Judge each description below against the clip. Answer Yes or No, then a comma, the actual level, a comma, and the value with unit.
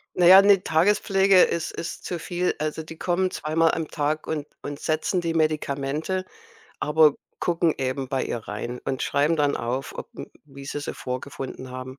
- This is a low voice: No, medium, 155 Hz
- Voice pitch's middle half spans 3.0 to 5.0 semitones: Yes, average, 3.9 semitones